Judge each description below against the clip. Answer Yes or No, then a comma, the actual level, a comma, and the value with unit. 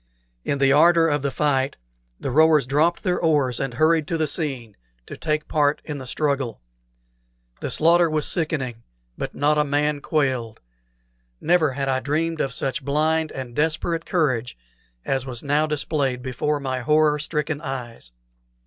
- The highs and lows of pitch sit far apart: No, average, 2.8 semitones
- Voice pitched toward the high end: No, medium, 145 Hz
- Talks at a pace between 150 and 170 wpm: Yes, average, 160 wpm